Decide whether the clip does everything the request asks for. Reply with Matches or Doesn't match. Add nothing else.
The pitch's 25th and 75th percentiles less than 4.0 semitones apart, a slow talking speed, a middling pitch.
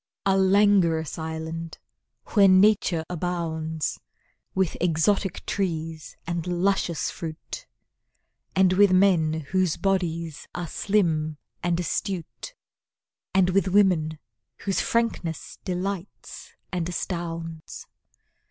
Matches